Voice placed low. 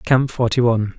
Yes: low, 120 Hz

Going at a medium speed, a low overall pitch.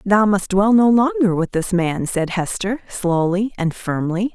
No: average, 180 wpm; high, 200 Hz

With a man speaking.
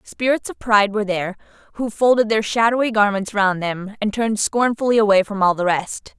No: female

